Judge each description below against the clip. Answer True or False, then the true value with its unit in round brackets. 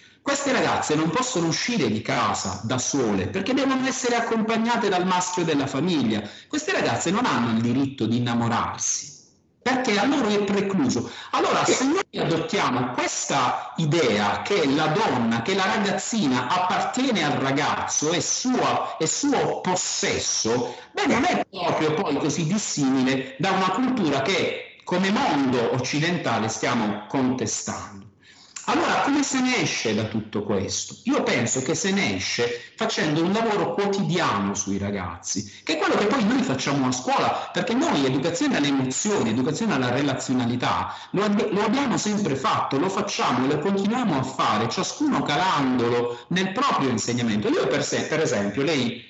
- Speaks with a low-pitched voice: False (165 Hz)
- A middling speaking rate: True (155 wpm)